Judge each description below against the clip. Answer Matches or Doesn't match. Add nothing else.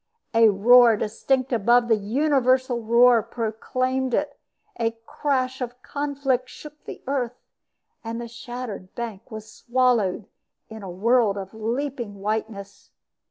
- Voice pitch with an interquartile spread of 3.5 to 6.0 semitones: Doesn't match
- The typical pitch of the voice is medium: Doesn't match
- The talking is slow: Matches